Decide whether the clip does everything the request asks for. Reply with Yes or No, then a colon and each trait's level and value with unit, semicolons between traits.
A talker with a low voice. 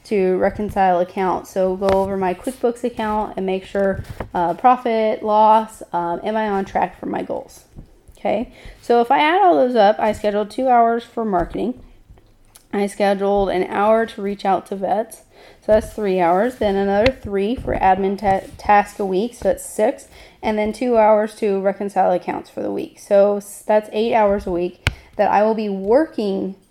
No: high, 205 Hz